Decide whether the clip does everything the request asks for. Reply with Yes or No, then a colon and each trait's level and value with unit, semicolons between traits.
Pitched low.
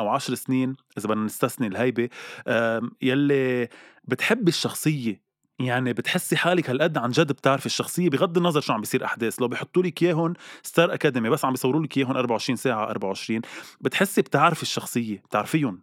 Yes: low, 130 Hz